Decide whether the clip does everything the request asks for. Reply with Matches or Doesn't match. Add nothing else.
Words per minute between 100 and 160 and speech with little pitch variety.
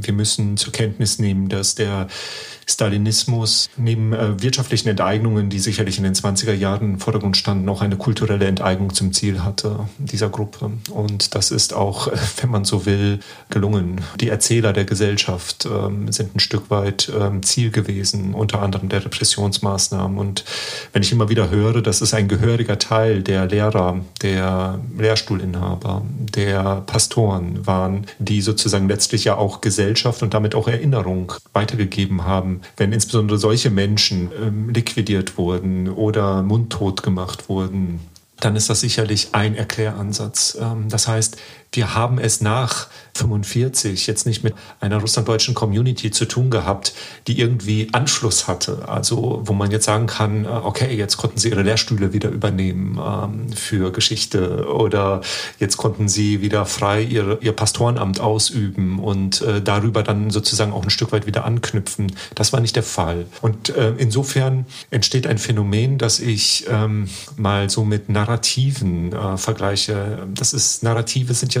Matches